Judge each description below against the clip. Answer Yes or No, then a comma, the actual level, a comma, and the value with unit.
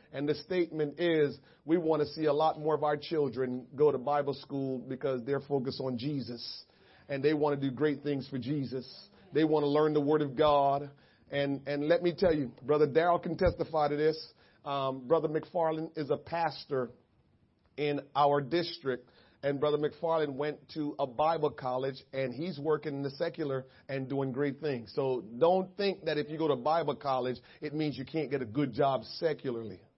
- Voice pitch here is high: No, medium, 145 Hz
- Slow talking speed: No, average, 195 wpm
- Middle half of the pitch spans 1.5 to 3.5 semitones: Yes, narrow, 2.5 semitones